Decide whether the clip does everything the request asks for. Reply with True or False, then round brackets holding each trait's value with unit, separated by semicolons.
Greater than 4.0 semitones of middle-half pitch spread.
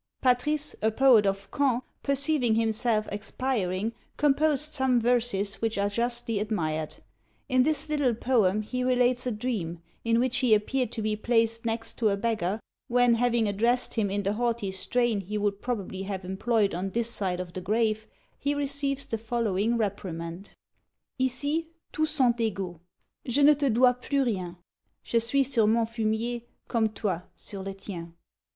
False (3.7 semitones)